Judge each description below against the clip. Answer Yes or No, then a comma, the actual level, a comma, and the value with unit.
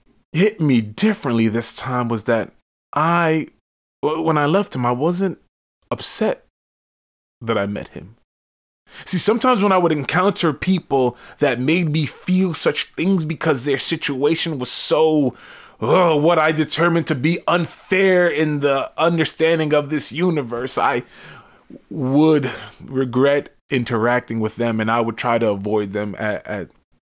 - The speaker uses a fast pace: No, average, 145 wpm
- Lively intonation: Yes, wide, 6.1 semitones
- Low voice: No, medium, 150 Hz